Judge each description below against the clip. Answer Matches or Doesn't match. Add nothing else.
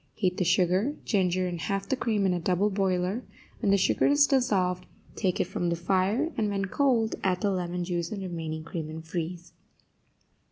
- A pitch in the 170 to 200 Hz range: Matches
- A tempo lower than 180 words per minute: Doesn't match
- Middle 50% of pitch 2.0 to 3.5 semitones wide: Matches